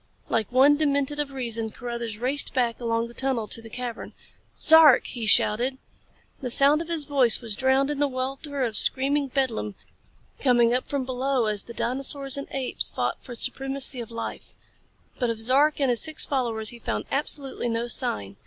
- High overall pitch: Yes, very high, 255 Hz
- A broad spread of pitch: No, average, 2.9 semitones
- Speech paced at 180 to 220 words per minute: Yes, average, 185 wpm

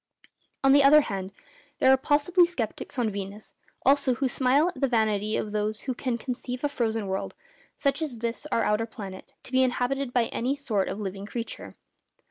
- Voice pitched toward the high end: Yes, high, 245 Hz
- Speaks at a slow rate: No, average, 190 wpm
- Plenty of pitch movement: No, average, 4.3 semitones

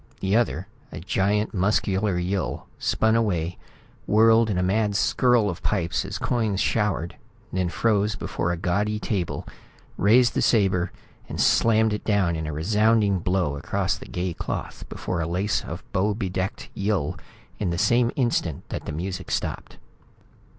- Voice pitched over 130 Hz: No, low, 100 Hz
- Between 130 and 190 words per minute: Yes, average, 155 wpm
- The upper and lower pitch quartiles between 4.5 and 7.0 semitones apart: No, average, 3.3 semitones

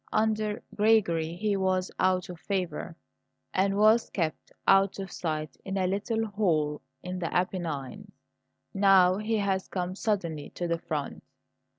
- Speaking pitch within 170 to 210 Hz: Yes, high, 190 Hz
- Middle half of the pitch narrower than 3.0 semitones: No, average, 3.3 semitones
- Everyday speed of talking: Yes, average, 145 wpm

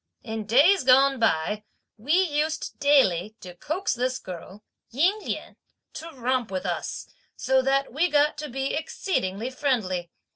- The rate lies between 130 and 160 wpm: Yes, average, 145 wpm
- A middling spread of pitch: No, wide, 5.7 semitones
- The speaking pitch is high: Yes, very high, 260 Hz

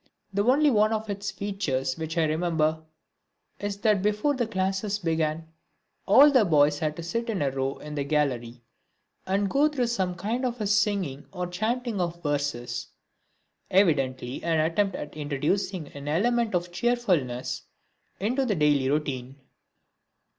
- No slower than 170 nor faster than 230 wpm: No, average, 150 wpm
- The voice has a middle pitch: Yes, medium, 180 Hz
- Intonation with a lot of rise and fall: Yes, wide, 6.0 semitones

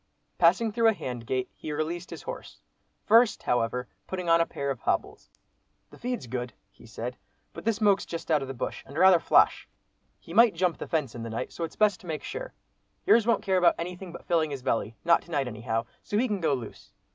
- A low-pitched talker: No, medium, 165 Hz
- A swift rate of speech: Yes, fast, 225 wpm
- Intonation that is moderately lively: No, wide, 7.4 semitones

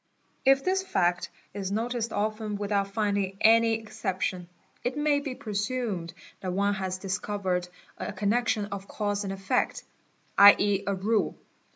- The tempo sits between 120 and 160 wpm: Yes, average, 140 wpm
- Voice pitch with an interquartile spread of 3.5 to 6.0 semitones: No, narrow, 2.5 semitones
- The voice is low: No, high, 205 Hz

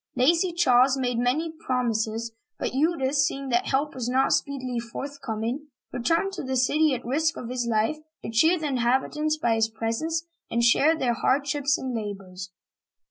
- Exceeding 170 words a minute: Yes, average, 180 wpm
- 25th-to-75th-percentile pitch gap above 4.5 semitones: No, average, 4.2 semitones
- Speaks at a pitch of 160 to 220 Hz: No, very high, 260 Hz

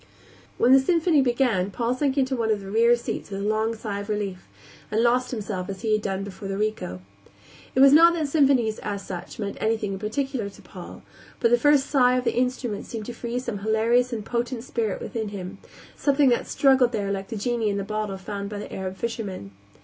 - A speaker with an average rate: No, fast, 220 wpm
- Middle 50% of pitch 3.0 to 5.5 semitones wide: Yes, average, 3.7 semitones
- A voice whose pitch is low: No, high, 225 Hz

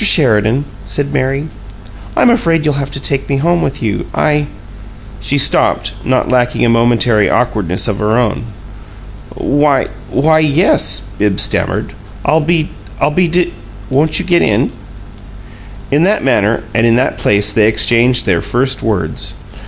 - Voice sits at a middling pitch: No, low, 130 Hz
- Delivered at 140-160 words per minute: Yes, average, 150 wpm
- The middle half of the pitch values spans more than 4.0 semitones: Yes, average, 5.2 semitones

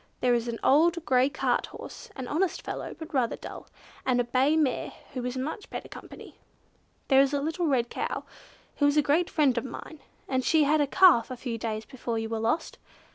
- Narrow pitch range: No, average, 4.1 semitones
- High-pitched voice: Yes, very high, 270 Hz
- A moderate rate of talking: No, fast, 215 wpm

